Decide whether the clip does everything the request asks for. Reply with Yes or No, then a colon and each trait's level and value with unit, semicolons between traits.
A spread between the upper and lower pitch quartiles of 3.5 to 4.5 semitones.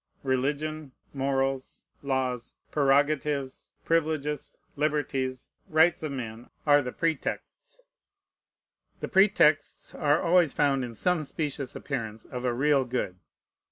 No: average, 2.8 semitones